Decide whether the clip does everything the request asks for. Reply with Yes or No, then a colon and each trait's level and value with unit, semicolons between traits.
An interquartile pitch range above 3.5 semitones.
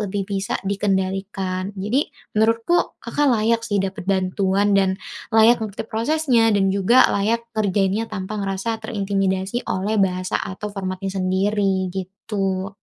No: narrow, 2.5 semitones